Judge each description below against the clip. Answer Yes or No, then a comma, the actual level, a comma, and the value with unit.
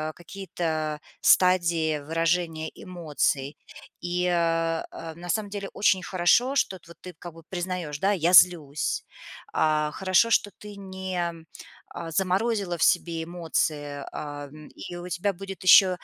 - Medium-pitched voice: Yes, medium, 175 Hz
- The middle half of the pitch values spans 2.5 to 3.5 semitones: Yes, average, 2.8 semitones